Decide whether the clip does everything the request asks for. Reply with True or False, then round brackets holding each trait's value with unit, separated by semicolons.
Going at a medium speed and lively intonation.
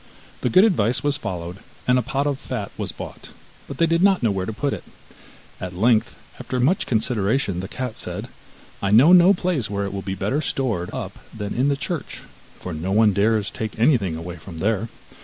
False (210 wpm; 6.2 semitones)